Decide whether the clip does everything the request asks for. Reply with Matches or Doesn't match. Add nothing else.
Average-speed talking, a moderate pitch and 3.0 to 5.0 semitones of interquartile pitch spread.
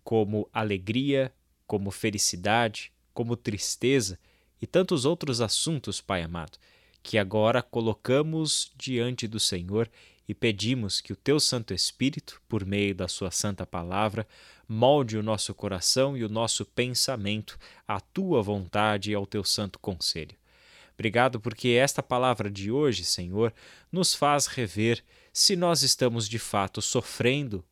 Doesn't match